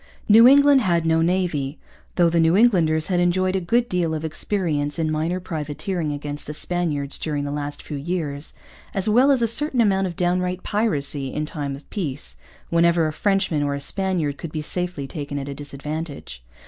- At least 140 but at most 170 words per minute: No, average, 190 wpm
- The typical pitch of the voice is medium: Yes, medium, 165 Hz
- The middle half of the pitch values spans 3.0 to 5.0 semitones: Yes, average, 4.1 semitones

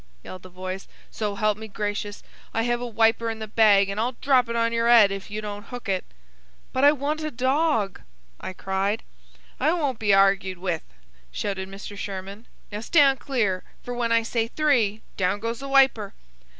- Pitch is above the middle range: Yes, high, 220 Hz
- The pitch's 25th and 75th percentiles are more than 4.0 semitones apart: No, average, 3.7 semitones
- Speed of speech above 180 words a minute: Yes, average, 190 wpm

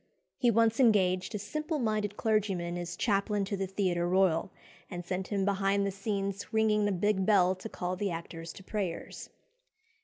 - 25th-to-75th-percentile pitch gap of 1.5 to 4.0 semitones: Yes, narrow, 2.5 semitones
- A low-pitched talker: No, high, 195 Hz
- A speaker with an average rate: Yes, average, 175 wpm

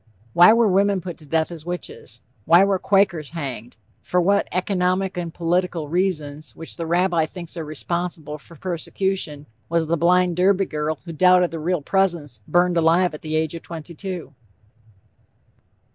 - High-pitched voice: No, medium, 170 Hz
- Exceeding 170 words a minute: No, average, 165 wpm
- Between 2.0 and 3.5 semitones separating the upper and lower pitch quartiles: Yes, narrow, 2.5 semitones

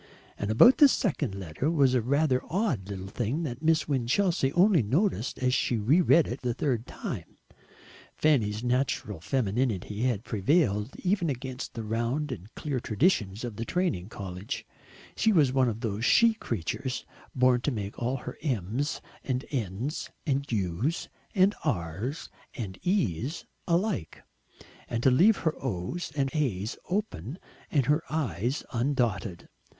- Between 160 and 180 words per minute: No, average, 150 wpm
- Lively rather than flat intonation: Yes, wide, 6.3 semitones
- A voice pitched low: Yes, low, 125 Hz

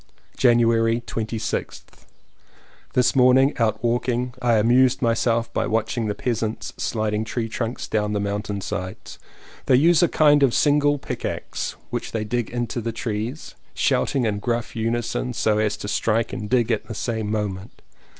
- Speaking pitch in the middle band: No, low, 115 Hz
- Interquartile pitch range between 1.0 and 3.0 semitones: Yes, narrow, 2.4 semitones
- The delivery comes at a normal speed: Yes, average, 160 wpm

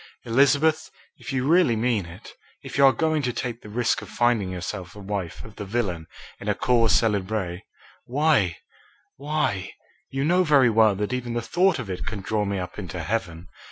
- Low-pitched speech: Yes, low, 115 Hz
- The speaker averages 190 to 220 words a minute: Yes, average, 195 wpm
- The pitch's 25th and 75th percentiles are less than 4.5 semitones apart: No, wide, 5.4 semitones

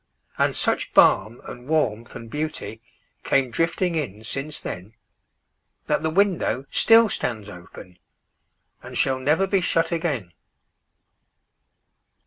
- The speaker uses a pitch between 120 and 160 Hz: Yes, low, 135 Hz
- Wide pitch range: Yes, wide, 6.8 semitones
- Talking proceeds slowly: Yes, slow, 105 wpm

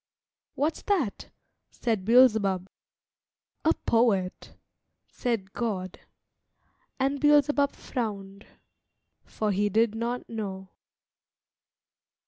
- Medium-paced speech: No, slow, 80 wpm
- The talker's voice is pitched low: No, high, 225 Hz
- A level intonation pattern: No, average, 4.4 semitones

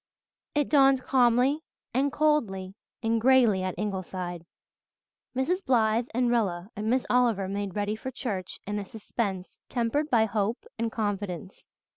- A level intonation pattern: No, average, 4.4 semitones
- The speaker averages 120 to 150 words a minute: Yes, average, 140 wpm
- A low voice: No, high, 225 Hz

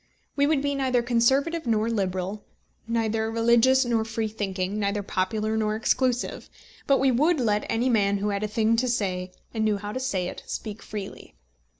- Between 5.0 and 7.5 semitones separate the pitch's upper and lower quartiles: No, average, 3.1 semitones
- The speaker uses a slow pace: No, average, 185 wpm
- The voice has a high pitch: Yes, high, 220 Hz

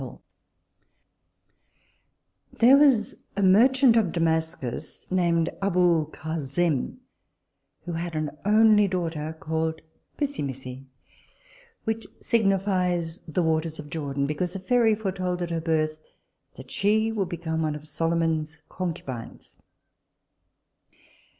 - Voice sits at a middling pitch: Yes, medium, 170 Hz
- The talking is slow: Yes, slow, 105 wpm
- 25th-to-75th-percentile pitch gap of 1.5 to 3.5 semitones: No, average, 3.9 semitones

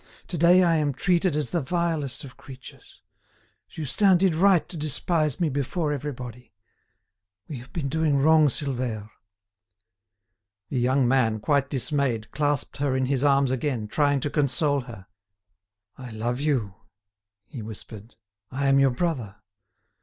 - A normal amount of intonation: Yes, average, 3.6 semitones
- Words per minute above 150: No, average, 145 wpm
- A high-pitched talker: No, medium, 140 Hz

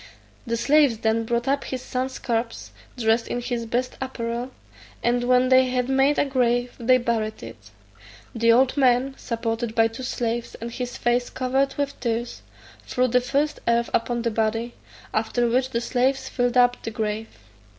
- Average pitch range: No, narrow, 1.8 semitones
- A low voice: No, high, 245 Hz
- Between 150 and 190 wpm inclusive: Yes, average, 170 wpm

